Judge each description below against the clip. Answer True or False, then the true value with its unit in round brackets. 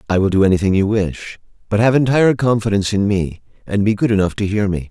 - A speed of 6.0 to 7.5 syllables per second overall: True (6.4 syllables/s)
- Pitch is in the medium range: False (105 Hz)